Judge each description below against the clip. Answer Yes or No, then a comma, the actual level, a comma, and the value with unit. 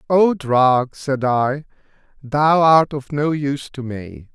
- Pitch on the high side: No, medium, 140 Hz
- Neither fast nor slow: Yes, average, 150 wpm